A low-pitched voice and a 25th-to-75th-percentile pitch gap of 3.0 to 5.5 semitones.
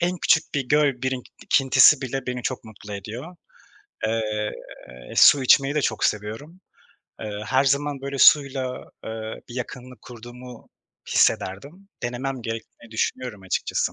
Yes: low, 125 Hz; average, 3.7 semitones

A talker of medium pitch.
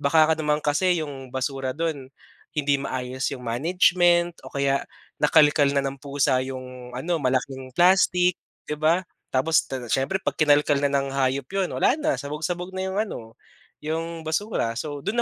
Yes: medium, 145 Hz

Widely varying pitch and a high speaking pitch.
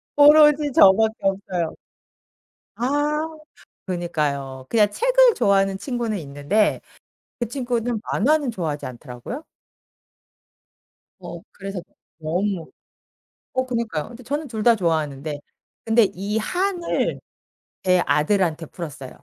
Yes: wide, 7.1 semitones; high, 205 Hz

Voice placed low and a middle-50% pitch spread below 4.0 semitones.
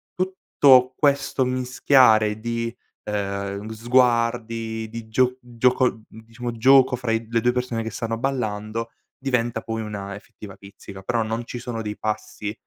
Yes: low, 115 Hz; narrow, 2.5 semitones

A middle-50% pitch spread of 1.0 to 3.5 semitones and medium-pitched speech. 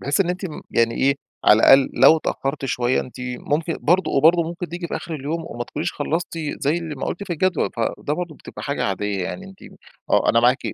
No: average, 4.3 semitones; medium, 155 Hz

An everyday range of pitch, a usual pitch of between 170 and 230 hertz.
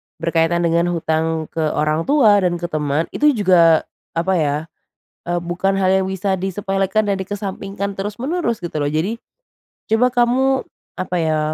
Yes: average, 3.7 semitones; high, 190 Hz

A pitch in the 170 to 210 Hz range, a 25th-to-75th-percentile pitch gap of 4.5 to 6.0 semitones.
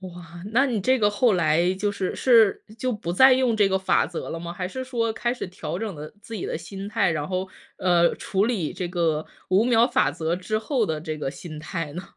Yes: high, 190 Hz; average, 4.9 semitones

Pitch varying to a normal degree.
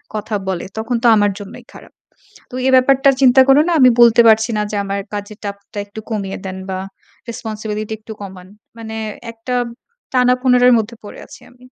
Yes: average, 3.3 semitones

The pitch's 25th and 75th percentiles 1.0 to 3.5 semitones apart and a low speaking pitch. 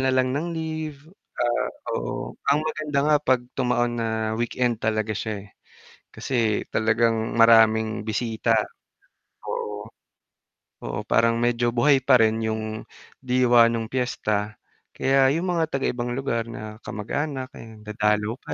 Yes: average, 3.1 semitones; low, 115 Hz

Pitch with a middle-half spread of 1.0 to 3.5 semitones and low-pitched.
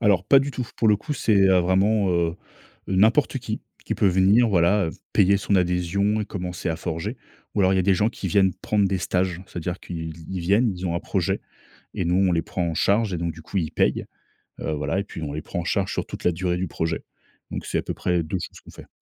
Yes: average, 2.8 semitones; very low, 95 Hz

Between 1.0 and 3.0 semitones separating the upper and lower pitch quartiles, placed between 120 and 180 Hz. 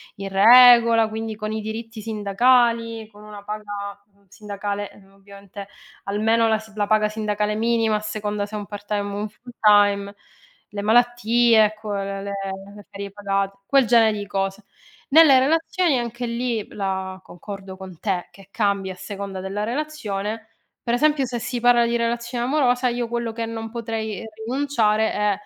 No: narrow, 2.6 semitones; high, 215 Hz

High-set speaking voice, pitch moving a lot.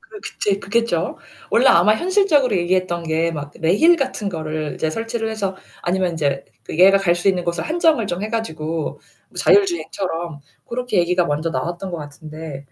No: medium, 180 Hz; wide, 5.7 semitones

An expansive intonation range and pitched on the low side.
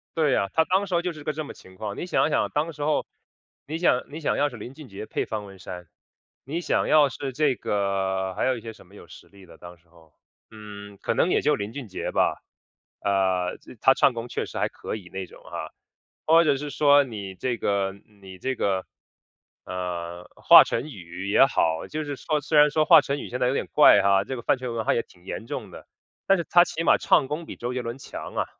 Yes: wide, 7.3 semitones; low, 120 Hz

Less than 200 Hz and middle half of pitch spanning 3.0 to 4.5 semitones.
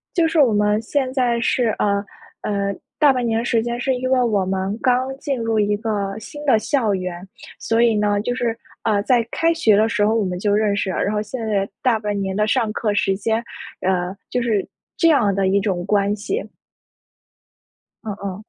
No: high, 215 Hz; average, 3.3 semitones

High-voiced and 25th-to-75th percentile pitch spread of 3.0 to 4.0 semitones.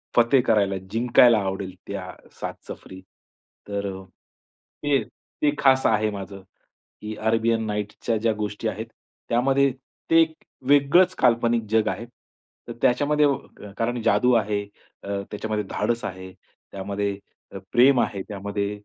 No: low, 110 Hz; average, 3.4 semitones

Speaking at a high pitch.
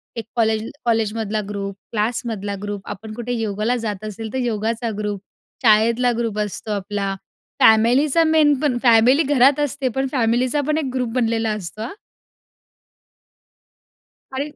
Yes: high, 225 Hz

